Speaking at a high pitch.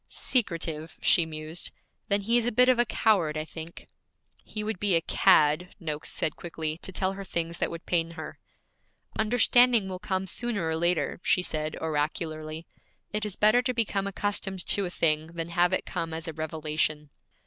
No: medium, 170 Hz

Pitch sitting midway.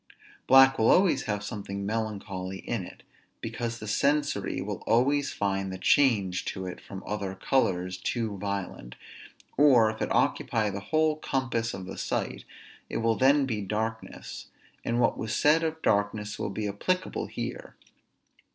No: low, 110 Hz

